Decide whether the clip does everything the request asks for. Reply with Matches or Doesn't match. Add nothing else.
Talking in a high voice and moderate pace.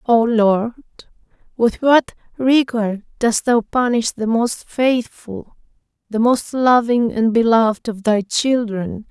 Doesn't match